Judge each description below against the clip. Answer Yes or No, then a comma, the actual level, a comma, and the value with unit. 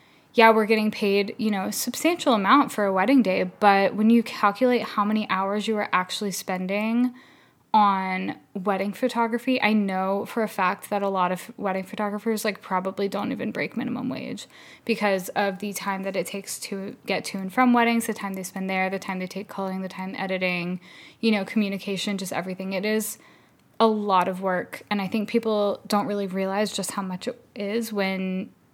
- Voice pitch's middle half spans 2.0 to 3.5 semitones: Yes, narrow, 2.6 semitones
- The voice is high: Yes, high, 205 Hz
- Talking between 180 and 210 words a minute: Yes, average, 200 wpm